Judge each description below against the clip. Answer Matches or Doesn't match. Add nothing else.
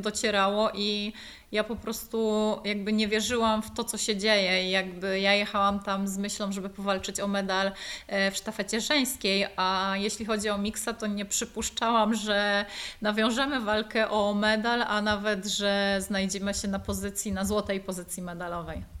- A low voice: Doesn't match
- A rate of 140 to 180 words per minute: Matches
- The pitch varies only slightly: Matches